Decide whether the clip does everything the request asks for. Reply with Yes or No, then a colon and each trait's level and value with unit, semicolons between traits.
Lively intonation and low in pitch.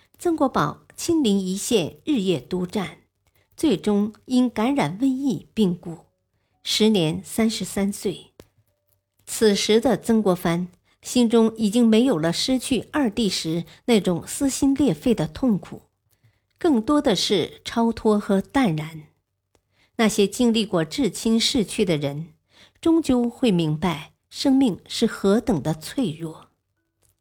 No: wide, 7.0 semitones; high, 205 Hz